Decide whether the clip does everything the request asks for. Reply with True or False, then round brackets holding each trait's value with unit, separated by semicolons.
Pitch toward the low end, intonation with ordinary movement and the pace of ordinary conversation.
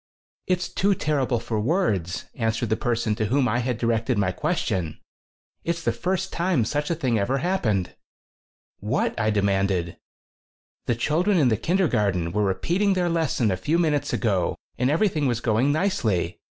False (120 Hz; 7.9 semitones; 170 wpm)